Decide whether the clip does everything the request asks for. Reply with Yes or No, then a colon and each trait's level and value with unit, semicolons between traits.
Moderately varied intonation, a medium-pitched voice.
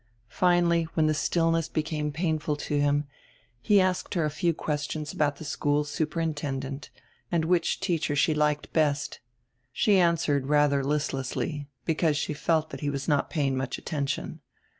No: narrow, 2.2 semitones; medium, 150 Hz